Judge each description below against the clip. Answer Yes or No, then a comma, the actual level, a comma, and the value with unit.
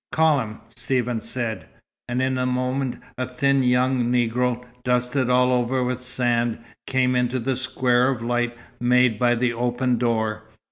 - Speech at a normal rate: Yes, average, 155 wpm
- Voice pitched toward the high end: No, low, 125 Hz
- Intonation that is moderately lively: No, narrow, 1.0 semitones